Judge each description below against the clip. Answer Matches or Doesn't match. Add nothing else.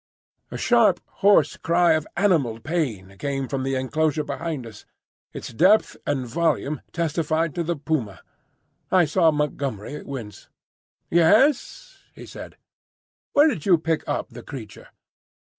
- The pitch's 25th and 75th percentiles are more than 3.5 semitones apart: Matches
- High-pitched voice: Doesn't match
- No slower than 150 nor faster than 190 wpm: Doesn't match